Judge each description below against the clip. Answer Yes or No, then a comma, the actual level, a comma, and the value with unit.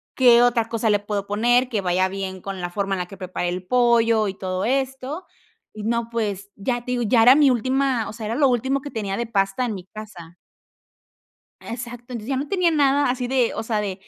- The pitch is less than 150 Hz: No, high, 230 Hz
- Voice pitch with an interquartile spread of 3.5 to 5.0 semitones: Yes, average, 4.1 semitones